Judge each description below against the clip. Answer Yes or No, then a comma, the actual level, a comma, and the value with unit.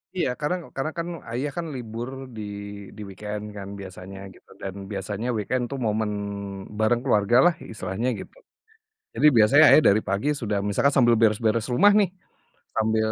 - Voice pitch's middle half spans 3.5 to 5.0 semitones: Yes, average, 4.2 semitones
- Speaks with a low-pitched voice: Yes, low, 110 Hz